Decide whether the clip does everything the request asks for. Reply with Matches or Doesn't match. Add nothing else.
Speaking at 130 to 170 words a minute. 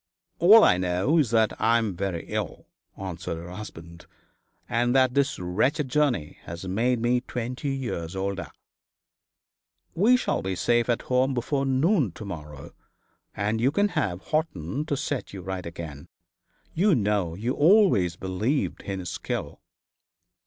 Matches